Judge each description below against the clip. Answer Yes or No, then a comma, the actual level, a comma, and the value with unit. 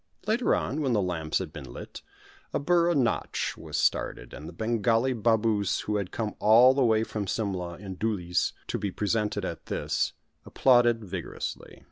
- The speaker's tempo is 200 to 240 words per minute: No, average, 170 wpm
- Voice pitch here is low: Yes, low, 110 Hz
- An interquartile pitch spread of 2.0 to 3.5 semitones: No, average, 4.1 semitones